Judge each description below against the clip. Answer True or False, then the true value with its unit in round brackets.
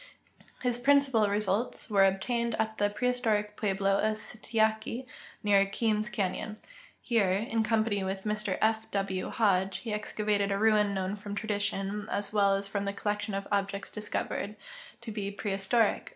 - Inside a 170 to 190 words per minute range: False (150 wpm)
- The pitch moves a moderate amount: False (1.7 semitones)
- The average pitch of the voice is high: True (210 Hz)